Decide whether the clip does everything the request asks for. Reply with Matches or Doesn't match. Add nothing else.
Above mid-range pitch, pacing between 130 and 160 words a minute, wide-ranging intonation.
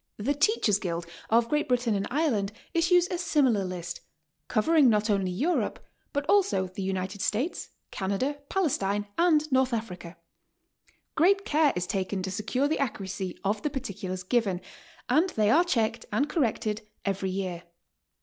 Matches